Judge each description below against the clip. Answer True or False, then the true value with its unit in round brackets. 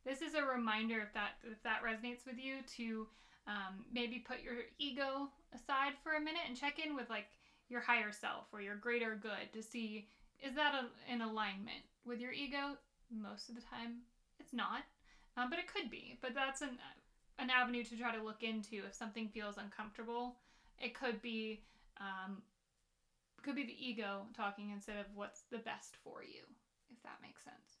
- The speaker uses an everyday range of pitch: True (3.2 semitones)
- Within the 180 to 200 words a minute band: True (190 wpm)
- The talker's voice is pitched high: True (240 Hz)